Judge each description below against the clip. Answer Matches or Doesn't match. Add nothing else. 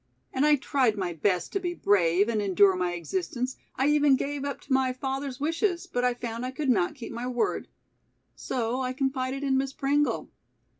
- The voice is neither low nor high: Doesn't match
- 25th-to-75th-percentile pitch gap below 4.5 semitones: Matches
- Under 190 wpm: Doesn't match